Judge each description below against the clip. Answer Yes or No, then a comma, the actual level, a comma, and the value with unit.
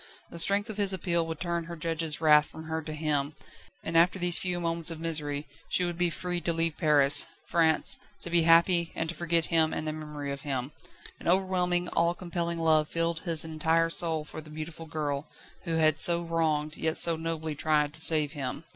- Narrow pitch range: Yes, narrow, 1.7 semitones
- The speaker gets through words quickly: Yes, fast, 210 wpm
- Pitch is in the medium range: Yes, medium, 165 Hz